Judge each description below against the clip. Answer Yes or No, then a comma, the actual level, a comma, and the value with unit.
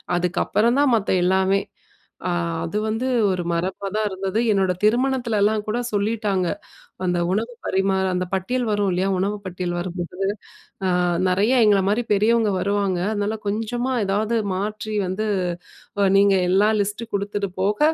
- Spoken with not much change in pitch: Yes, narrow, 2.3 semitones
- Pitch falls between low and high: No, high, 200 Hz